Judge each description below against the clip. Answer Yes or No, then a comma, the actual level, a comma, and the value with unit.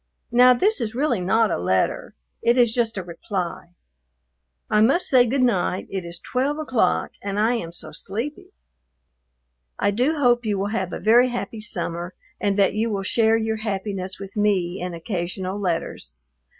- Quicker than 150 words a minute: Yes, average, 175 wpm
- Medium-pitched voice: No, high, 210 Hz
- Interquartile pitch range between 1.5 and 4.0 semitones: No, average, 4.4 semitones